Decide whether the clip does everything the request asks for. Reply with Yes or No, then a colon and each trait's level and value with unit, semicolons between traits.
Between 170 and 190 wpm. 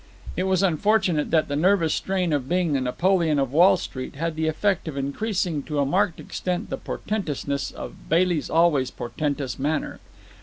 Yes: average, 180 wpm